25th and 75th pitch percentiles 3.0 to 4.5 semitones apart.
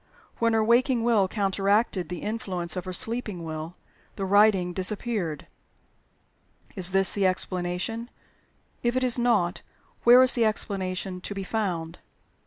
Yes: average, 4.0 semitones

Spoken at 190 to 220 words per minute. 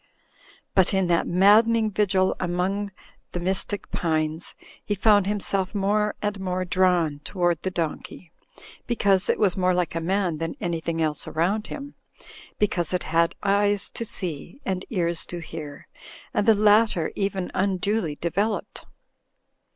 No: average, 150 wpm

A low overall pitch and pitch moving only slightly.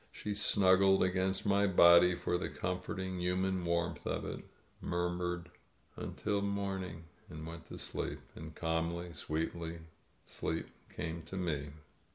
Yes: very low, 90 Hz; narrow, 2.2 semitones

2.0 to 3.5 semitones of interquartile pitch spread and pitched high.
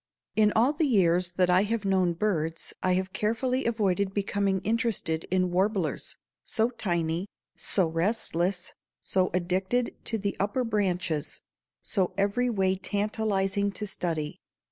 Yes: average, 3.1 semitones; high, 195 Hz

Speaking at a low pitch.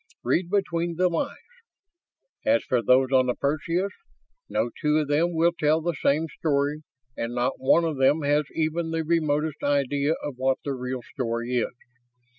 No: medium, 150 Hz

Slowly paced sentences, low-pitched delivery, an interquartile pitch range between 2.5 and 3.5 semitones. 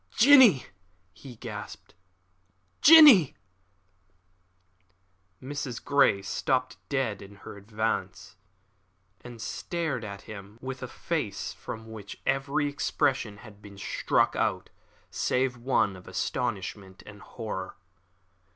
No: slow, 105 wpm; low, 115 Hz; average, 5.1 semitones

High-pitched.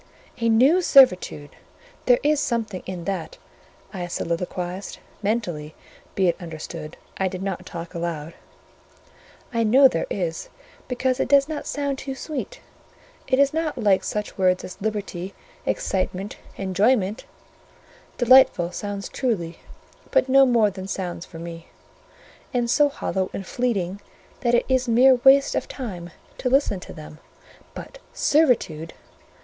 Yes: high, 205 Hz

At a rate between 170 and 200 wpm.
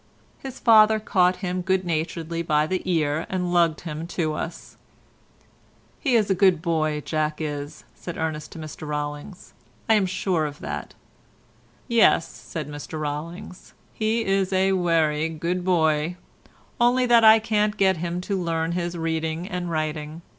No: average, 145 wpm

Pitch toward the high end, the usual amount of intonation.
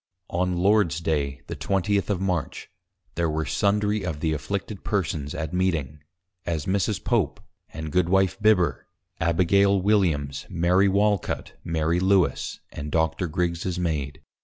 No: very low, 90 Hz; average, 3.7 semitones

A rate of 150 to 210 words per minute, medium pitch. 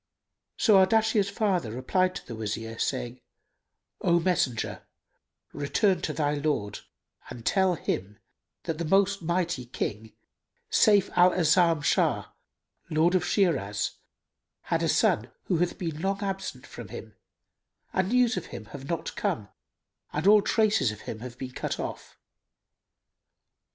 No: average, 140 wpm; medium, 170 Hz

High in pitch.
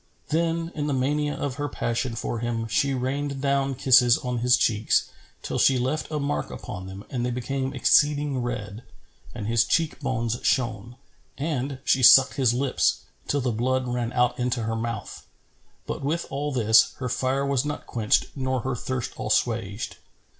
No: low, 130 Hz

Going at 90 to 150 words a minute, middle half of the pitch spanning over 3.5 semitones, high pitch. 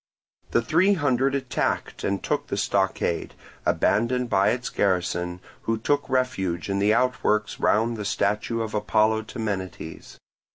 No: slow, 135 wpm; average, 4.1 semitones; low, 110 Hz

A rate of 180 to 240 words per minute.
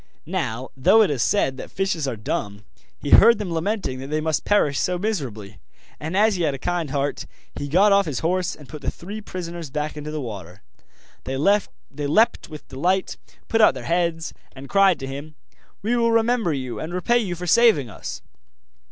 Yes: average, 195 wpm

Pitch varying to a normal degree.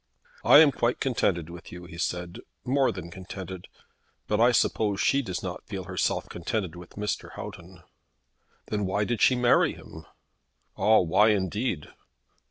Yes: average, 4.2 semitones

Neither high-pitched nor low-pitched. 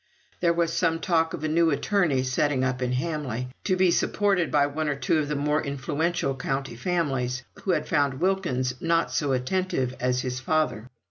Yes: medium, 145 Hz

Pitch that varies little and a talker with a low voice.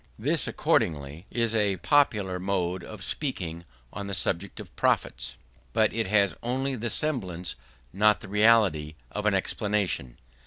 No: average, 3.7 semitones; low, 100 Hz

